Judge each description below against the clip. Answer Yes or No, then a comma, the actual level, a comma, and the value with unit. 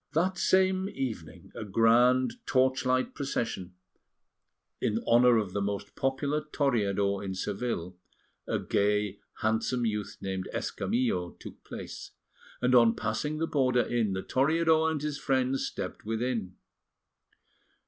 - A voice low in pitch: Yes, low, 120 Hz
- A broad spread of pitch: No, average, 4.8 semitones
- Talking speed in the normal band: No, slow, 125 wpm